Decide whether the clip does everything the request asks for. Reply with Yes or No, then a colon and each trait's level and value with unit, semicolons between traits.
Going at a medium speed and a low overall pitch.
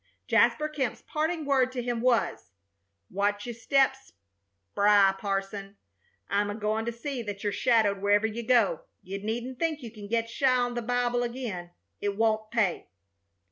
No: average, 160 wpm; high, 230 Hz